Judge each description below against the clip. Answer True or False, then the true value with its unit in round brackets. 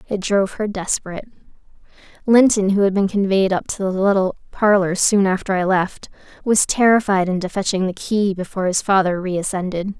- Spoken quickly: False (175 wpm)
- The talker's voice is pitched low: False (195 Hz)